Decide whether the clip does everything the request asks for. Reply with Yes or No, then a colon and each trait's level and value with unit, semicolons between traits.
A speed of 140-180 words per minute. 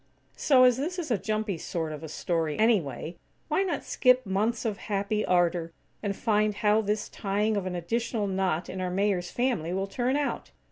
No: average, 190 wpm